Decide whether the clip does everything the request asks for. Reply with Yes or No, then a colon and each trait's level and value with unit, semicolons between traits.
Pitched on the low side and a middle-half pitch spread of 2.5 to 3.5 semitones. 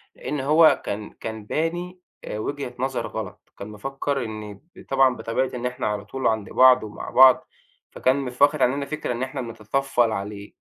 No: low, 130 Hz; average, 4.1 semitones